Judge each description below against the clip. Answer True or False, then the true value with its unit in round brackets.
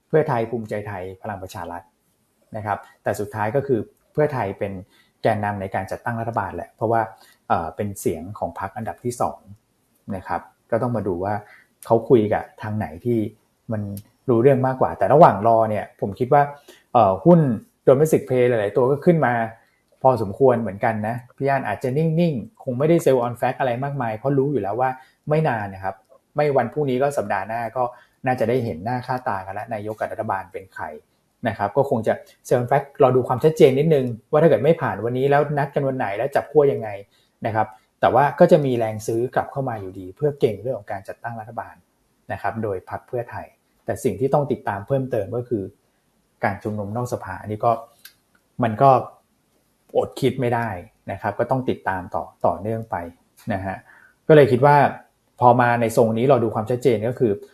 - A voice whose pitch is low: True (120 Hz)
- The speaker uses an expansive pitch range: False (4.0 semitones)